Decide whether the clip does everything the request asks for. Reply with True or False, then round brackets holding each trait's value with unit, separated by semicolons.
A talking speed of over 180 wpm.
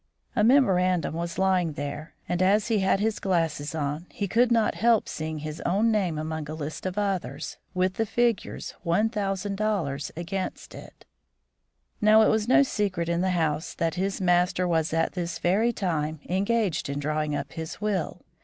False (175 wpm)